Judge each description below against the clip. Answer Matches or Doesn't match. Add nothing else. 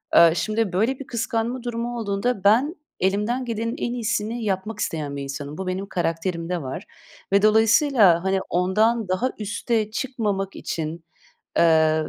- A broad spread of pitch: Doesn't match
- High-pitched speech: Matches